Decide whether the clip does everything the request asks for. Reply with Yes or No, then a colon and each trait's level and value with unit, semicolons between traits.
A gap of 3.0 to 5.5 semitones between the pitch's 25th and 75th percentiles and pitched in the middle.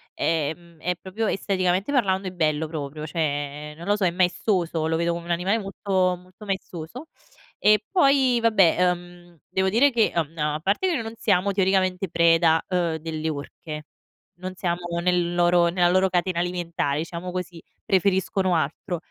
No: narrow, 2.5 semitones; medium, 180 Hz